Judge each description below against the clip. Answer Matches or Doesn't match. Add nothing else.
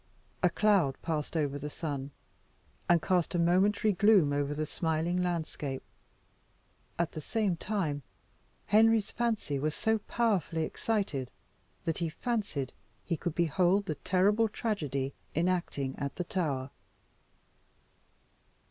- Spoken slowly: Matches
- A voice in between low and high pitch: Matches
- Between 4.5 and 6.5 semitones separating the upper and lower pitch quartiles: Matches